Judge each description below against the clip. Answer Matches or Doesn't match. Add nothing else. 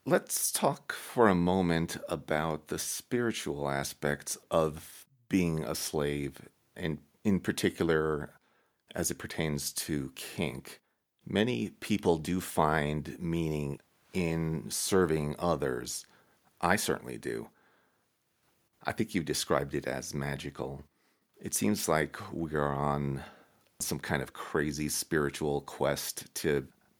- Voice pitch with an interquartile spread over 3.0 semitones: Doesn't match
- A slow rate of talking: Matches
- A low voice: Matches